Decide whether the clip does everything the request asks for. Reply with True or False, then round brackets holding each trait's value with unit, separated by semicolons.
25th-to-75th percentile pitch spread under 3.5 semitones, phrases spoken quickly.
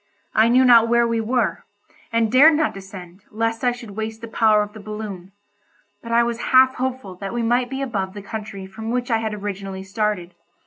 True (2.8 semitones; 210 wpm)